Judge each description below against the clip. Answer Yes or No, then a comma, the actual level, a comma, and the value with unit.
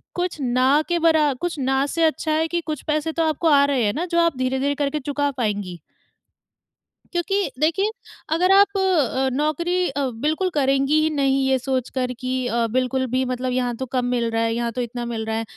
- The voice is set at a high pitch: Yes, very high, 275 Hz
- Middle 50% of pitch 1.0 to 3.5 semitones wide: No, average, 4.1 semitones